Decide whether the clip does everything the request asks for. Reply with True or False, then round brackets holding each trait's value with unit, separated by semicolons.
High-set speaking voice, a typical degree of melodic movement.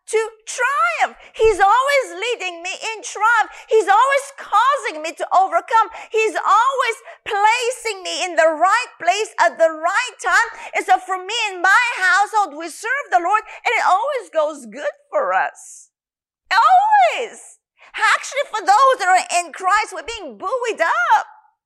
True (400 Hz; 4.2 semitones)